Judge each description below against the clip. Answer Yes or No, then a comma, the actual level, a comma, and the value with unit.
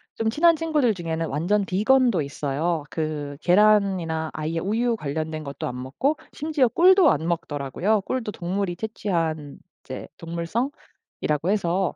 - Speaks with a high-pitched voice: No, medium, 175 Hz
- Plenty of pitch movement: Yes, wide, 6.0 semitones